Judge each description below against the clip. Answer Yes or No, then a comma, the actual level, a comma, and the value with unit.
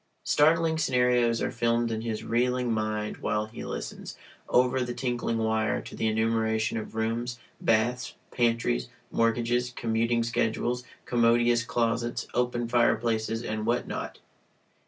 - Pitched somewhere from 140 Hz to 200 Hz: No, low, 115 Hz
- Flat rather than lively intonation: Yes, narrow, 1.6 semitones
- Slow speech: Yes, slow, 130 wpm